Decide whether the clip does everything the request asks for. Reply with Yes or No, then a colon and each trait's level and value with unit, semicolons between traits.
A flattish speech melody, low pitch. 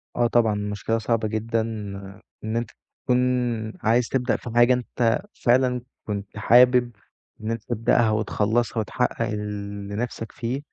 Yes: narrow, 2.2 semitones; low, 115 Hz